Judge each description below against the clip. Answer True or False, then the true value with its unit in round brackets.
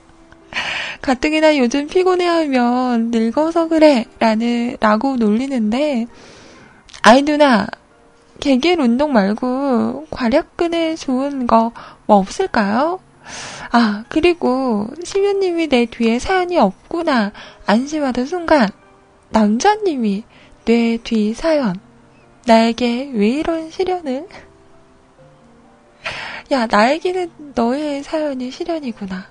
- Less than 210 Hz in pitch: False (260 Hz)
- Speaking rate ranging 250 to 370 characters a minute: False (205 characters per minute)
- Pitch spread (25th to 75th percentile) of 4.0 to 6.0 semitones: True (5.5 semitones)